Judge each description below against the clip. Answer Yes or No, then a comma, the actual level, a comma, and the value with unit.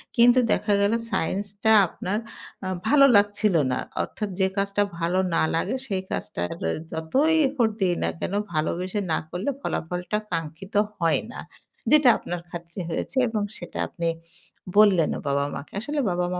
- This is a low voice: No, high, 190 Hz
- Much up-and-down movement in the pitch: No, average, 4.0 semitones